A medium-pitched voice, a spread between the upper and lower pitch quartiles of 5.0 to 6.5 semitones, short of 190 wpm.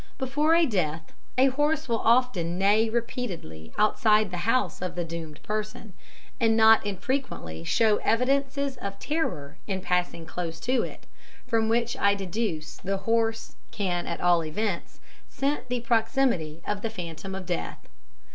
No: high, 215 Hz; average, 5.3 semitones; average, 150 wpm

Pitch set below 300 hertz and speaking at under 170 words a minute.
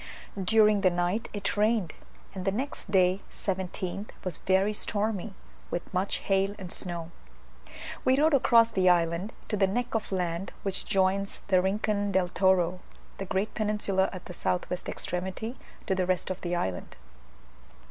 Yes: high, 190 Hz; average, 160 wpm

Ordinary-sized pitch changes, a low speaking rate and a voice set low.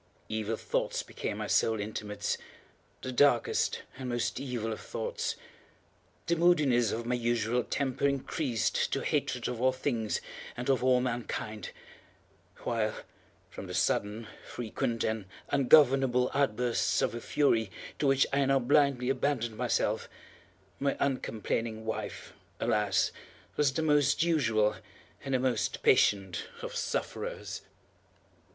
Yes: average, 3.6 semitones; slow, 125 wpm; low, 120 Hz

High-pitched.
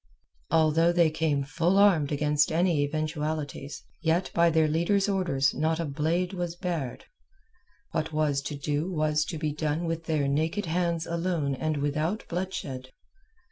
No: medium, 160 Hz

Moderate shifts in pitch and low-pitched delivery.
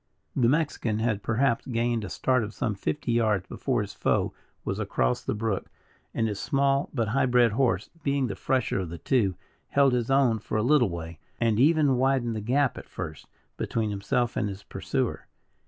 Yes: average, 4.2 semitones; low, 115 Hz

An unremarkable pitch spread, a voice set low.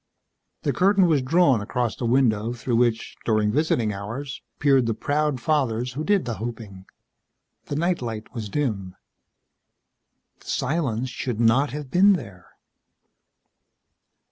Yes: average, 4.8 semitones; low, 125 Hz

